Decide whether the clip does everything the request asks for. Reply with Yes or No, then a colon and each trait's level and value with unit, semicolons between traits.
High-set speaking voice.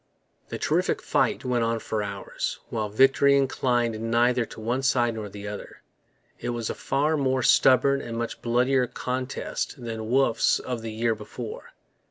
No: low, 120 Hz